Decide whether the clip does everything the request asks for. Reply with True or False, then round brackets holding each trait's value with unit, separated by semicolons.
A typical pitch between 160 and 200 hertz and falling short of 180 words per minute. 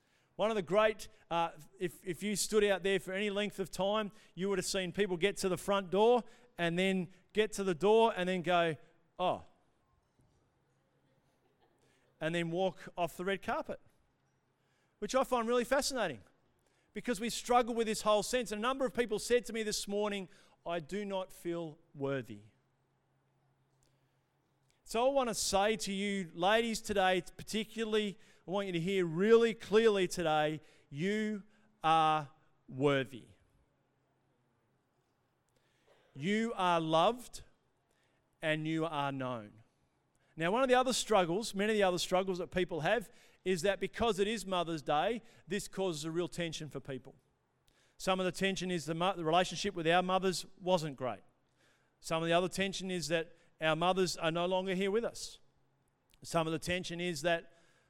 True (185 Hz; 165 wpm)